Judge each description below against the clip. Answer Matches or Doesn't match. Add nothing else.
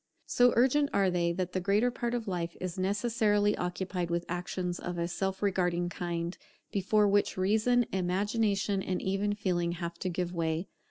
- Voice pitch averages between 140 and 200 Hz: Matches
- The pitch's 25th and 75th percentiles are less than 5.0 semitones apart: Matches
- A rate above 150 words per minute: Matches